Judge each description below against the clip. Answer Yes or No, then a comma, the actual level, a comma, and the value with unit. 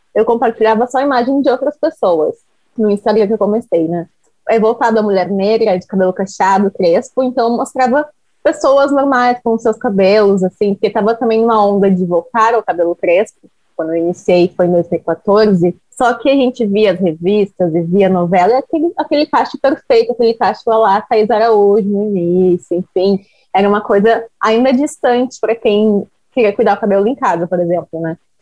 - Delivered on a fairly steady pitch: No, average, 4.6 semitones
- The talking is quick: No, average, 175 wpm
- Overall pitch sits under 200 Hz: No, high, 215 Hz